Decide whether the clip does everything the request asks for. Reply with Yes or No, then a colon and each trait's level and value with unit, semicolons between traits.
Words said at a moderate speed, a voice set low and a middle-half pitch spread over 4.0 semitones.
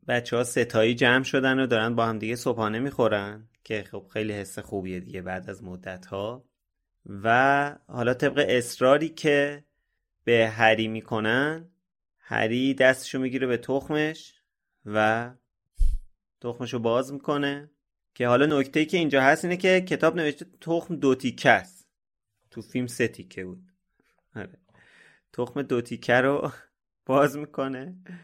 Yes: average, 140 wpm; low, 125 Hz; average, 4.4 semitones